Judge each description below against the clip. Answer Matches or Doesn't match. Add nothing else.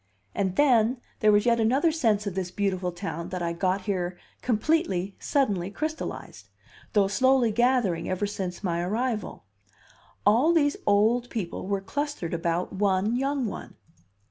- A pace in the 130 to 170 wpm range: Matches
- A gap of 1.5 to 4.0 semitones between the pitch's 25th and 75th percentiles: Doesn't match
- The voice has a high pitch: Matches